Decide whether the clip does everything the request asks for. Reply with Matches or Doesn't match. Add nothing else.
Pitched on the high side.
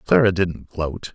Doesn't match